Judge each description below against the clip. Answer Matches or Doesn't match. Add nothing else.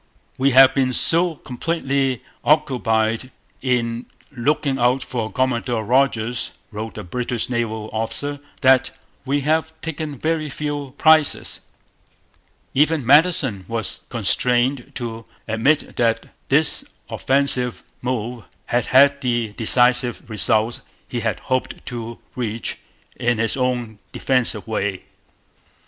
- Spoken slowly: Matches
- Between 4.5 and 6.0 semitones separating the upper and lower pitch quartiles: Doesn't match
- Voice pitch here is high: Doesn't match